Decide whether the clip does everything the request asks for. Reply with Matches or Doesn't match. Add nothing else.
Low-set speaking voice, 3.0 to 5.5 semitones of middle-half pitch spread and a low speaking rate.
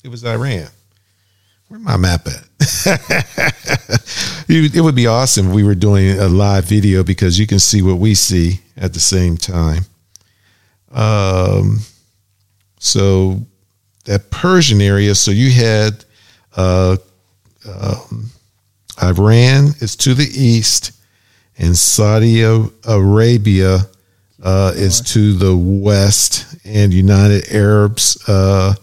Doesn't match